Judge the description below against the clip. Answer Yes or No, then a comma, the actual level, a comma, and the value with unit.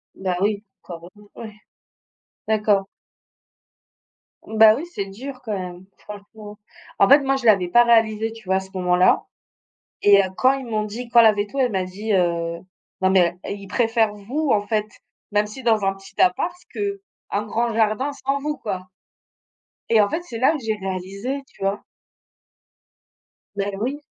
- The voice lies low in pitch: No, high, 210 Hz